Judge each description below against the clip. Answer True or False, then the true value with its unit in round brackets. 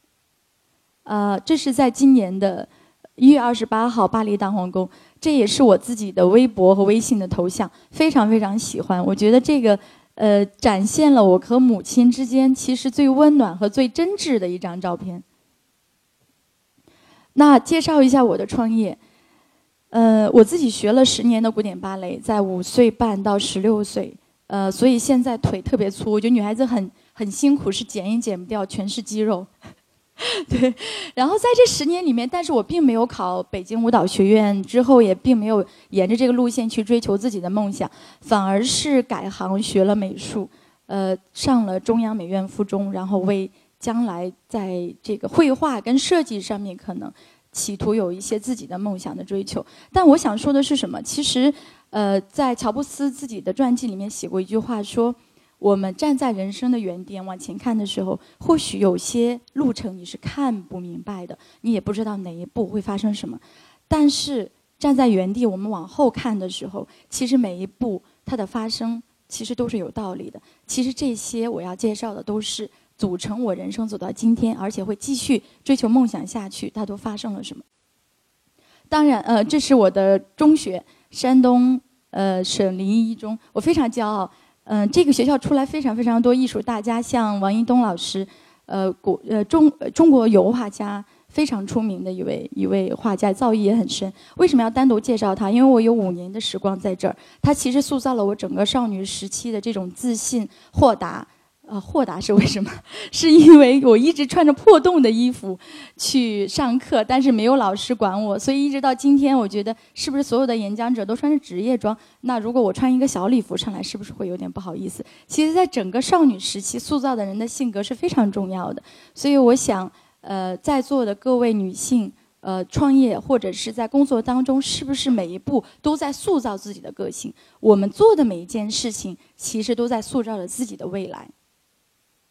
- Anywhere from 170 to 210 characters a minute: False (285 characters per minute)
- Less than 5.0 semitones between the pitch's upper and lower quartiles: True (4.6 semitones)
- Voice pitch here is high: True (230 Hz)